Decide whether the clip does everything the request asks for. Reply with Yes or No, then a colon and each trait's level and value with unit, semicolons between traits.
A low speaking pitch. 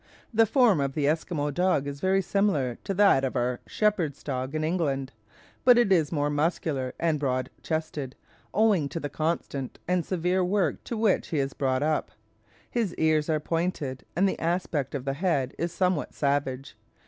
No: medium, 155 Hz